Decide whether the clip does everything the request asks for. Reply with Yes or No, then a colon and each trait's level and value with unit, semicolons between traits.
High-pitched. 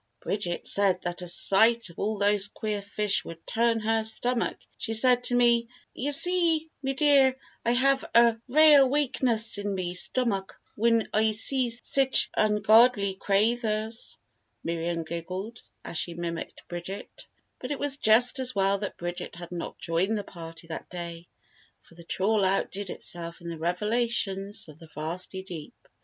Yes: high, 210 Hz